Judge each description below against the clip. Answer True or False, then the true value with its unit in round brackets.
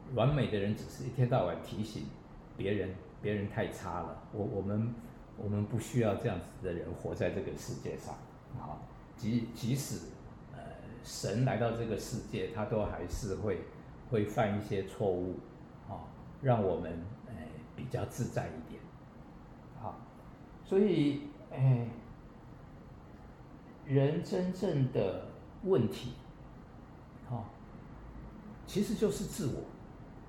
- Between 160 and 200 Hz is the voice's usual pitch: False (120 Hz)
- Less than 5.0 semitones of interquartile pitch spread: True (4.3 semitones)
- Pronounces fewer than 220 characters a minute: True (185 characters per minute)